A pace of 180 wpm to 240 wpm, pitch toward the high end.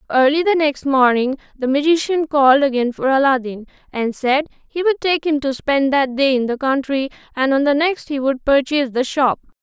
Yes: average, 200 wpm; very high, 280 Hz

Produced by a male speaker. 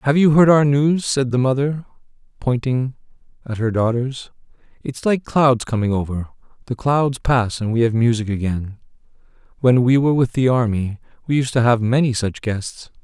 Yes: male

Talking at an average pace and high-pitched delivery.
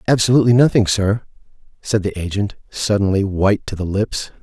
No: average, 150 wpm; low, 105 Hz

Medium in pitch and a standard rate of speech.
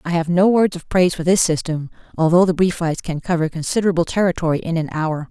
No: medium, 170 Hz; fast, 215 wpm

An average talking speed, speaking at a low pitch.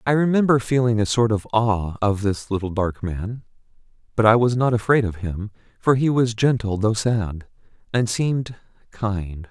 Yes: average, 170 wpm; low, 110 Hz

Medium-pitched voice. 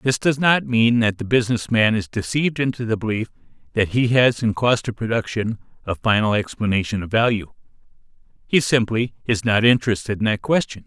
No: low, 115 Hz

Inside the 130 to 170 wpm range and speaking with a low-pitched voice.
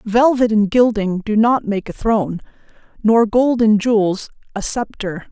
No: average, 160 wpm; high, 215 Hz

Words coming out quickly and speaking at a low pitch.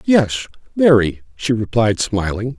No: slow, 95 wpm; low, 120 Hz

